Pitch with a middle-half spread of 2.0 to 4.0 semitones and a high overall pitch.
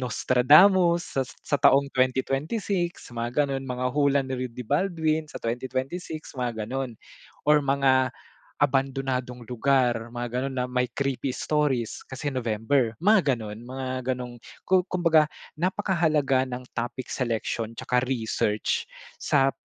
No: average, 3.2 semitones; low, 130 Hz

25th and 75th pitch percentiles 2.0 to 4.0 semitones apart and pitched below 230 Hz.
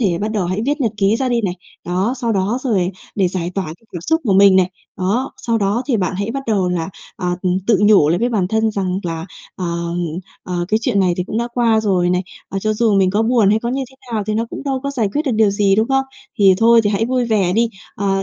Yes: average, 3.7 semitones; high, 205 Hz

